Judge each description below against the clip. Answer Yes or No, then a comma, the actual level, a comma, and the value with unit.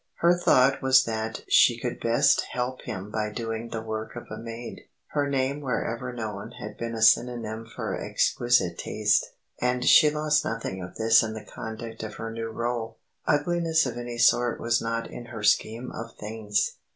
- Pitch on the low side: Yes, low, 115 Hz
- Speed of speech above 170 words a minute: Yes, average, 180 wpm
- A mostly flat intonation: Yes, narrow, 2.1 semitones